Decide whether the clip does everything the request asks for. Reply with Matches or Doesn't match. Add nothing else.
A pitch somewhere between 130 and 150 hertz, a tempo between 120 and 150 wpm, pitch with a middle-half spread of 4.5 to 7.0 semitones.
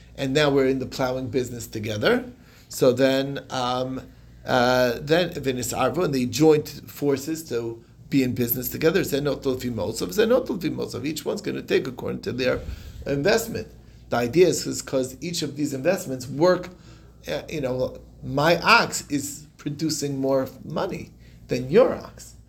Doesn't match